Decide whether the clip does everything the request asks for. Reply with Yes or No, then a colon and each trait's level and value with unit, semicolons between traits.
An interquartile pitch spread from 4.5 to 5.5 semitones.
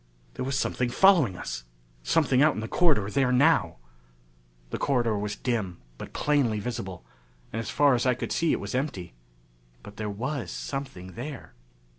Yes: average, 5.1 semitones